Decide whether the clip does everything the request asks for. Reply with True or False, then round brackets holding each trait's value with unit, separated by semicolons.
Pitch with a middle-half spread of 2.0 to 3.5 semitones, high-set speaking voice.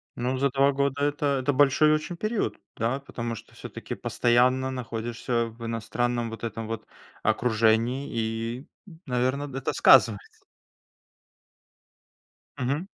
False (3.2 semitones; 125 Hz)